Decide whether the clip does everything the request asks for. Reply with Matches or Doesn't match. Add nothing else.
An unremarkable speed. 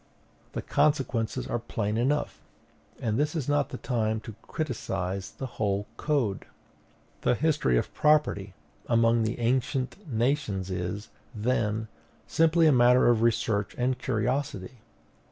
Doesn't match